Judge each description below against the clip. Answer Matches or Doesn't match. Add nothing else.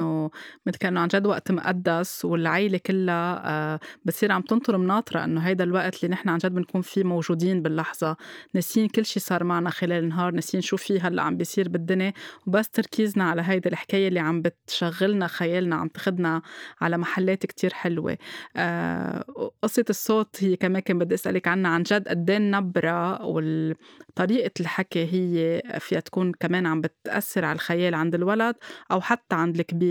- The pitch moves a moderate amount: Doesn't match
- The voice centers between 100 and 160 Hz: Doesn't match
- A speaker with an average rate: Doesn't match